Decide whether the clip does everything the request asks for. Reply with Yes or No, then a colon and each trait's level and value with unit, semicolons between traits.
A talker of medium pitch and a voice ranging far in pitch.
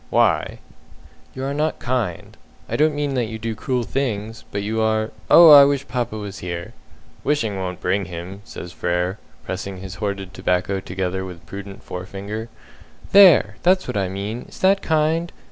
No: low, 105 Hz; wide, 6.0 semitones